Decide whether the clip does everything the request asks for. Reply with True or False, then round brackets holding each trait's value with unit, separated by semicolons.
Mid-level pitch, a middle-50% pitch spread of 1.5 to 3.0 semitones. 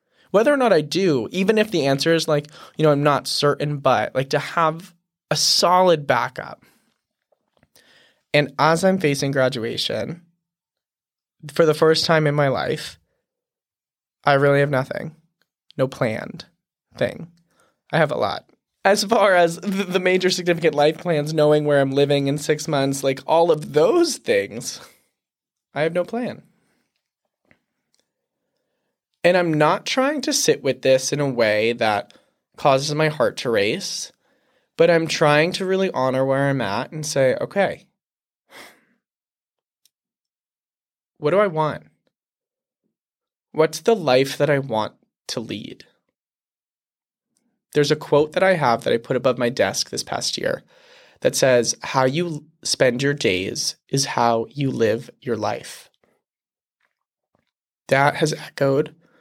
False (155 Hz; 4.1 semitones)